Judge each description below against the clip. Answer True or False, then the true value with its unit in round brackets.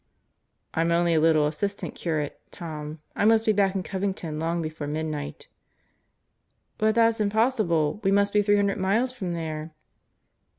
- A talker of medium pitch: True (175 Hz)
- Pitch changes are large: False (4.6 semitones)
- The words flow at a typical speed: True (155 wpm)